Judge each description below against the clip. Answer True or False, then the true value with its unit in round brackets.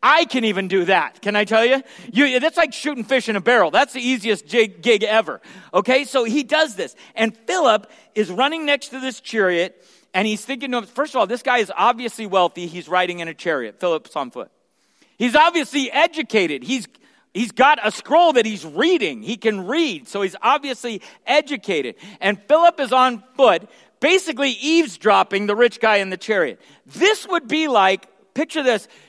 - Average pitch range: False (5.8 semitones)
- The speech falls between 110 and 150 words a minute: False (190 wpm)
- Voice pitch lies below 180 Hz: False (245 Hz)